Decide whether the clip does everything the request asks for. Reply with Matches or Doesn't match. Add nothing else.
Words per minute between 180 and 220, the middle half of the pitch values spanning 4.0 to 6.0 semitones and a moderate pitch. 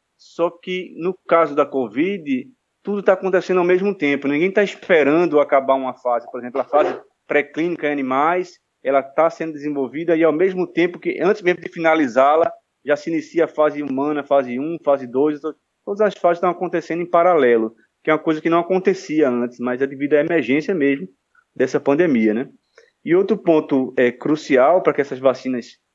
Matches